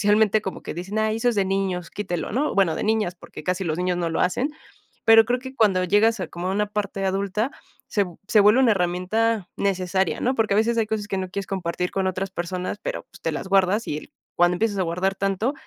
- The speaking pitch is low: No, high, 195 Hz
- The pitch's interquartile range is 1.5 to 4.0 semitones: Yes, average, 3.0 semitones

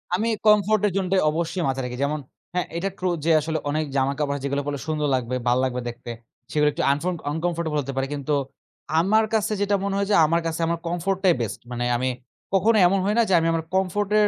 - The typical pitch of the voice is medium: Yes, medium, 165 Hz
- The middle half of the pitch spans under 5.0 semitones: No, wide, 5.4 semitones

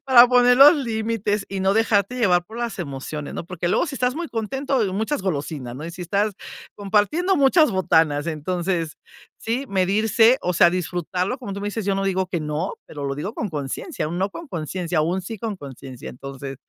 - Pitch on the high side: Yes, high, 195 Hz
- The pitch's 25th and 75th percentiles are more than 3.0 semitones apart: Yes, wide, 5.6 semitones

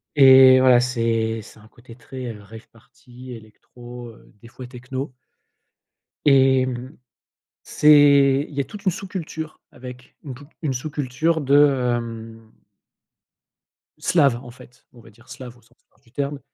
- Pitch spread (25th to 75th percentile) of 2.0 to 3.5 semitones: Yes, average, 2.8 semitones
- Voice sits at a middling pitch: No, low, 130 Hz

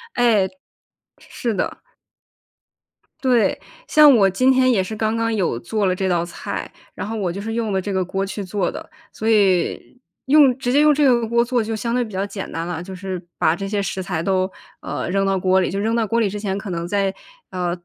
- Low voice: No, high, 200 Hz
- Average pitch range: Yes, average, 3.5 semitones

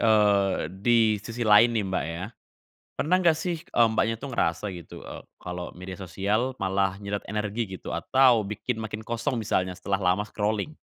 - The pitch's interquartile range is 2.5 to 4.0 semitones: Yes, average, 3.1 semitones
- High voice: No, low, 105 Hz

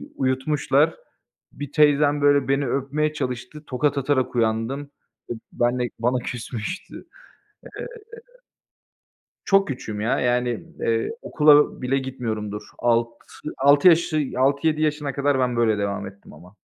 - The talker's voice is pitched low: Yes, low, 130 Hz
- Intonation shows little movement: No, average, 3.4 semitones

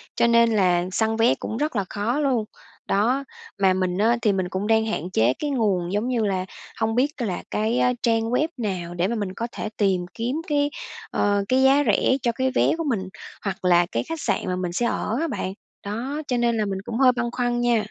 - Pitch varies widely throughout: No, average, 4.4 semitones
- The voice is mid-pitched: No, high, 225 Hz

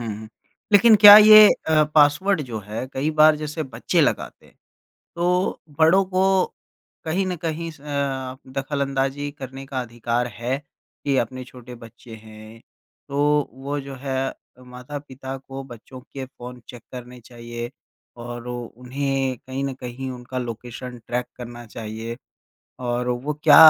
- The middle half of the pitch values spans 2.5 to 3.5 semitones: Yes, average, 3.2 semitones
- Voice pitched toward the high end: No, low, 130 Hz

